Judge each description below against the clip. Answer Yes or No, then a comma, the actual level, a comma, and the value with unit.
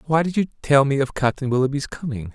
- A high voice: No, medium, 140 Hz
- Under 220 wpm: No, fast, 230 wpm